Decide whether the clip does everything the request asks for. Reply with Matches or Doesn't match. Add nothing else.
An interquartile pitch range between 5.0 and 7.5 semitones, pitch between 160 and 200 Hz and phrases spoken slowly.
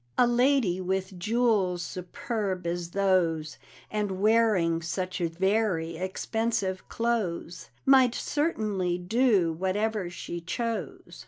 Doesn't match